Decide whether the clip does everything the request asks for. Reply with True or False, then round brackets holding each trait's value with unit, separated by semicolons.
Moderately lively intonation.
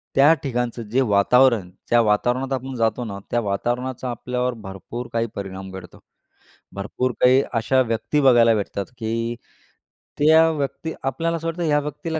True (3.2 semitones)